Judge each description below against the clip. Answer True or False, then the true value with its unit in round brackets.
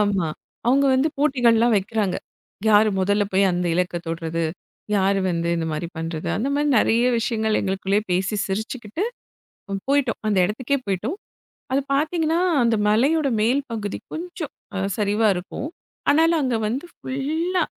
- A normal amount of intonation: False (6.2 semitones)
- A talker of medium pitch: False (220 Hz)